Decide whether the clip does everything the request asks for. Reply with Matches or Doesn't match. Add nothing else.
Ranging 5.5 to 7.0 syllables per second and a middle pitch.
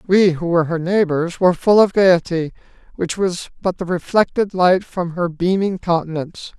Doesn't match